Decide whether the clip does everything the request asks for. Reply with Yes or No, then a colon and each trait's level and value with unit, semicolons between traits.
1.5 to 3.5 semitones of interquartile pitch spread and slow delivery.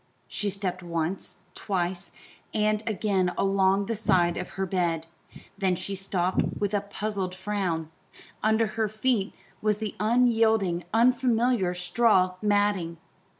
Yes: average, 2.9 semitones; slow, 125 wpm